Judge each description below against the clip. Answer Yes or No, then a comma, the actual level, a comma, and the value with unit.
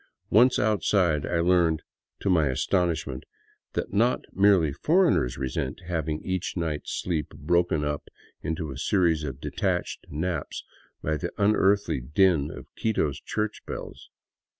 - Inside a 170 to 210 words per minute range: No, average, 140 wpm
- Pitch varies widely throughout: No, average, 4.4 semitones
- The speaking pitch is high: No, very low, 85 Hz